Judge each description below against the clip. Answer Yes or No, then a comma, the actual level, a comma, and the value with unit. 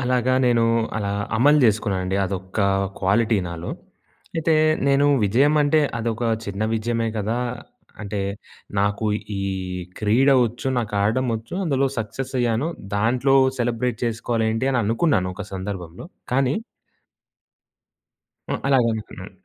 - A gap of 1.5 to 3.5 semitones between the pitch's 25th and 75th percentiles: No, average, 3.9 semitones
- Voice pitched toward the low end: Yes, low, 115 Hz